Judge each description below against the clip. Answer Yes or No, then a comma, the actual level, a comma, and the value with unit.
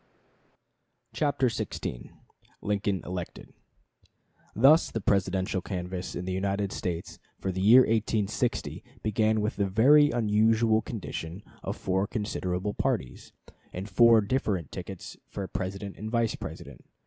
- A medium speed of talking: No, slow, 125 wpm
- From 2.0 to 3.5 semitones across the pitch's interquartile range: Yes, average, 3.1 semitones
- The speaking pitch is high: No, low, 100 Hz